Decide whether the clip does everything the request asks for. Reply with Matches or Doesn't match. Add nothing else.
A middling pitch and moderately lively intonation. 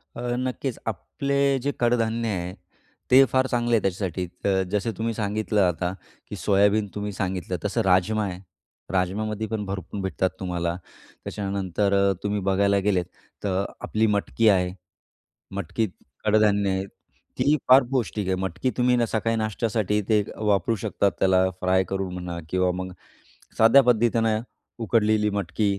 Doesn't match